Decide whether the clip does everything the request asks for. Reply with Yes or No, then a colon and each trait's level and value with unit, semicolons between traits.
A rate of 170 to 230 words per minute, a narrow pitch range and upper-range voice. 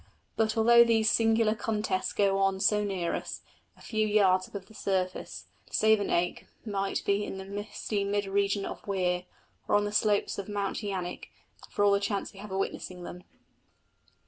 Yes: average, 175 wpm; narrow, 1.7 semitones; high, 200 Hz